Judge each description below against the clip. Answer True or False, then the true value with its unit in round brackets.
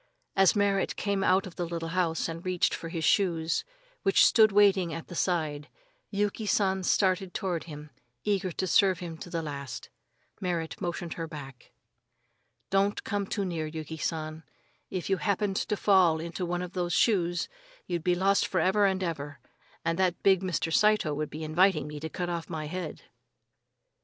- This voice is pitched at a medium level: True (175 Hz)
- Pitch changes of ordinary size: True (3.0 semitones)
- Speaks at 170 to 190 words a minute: True (180 wpm)